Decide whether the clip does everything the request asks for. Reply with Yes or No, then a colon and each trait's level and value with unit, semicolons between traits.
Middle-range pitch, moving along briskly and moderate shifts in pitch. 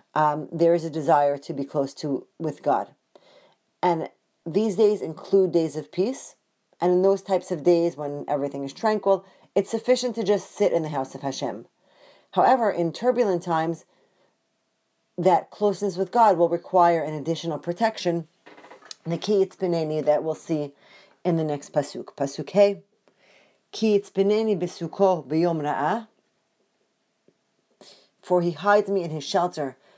No: medium, 175 Hz; average, 150 wpm; average, 4.4 semitones